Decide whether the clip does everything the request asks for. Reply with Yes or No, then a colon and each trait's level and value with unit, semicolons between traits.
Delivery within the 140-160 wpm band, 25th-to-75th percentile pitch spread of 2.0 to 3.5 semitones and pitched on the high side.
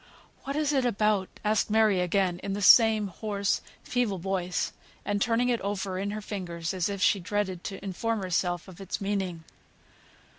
No: average, 175 wpm; narrow, 2.5 semitones; high, 200 Hz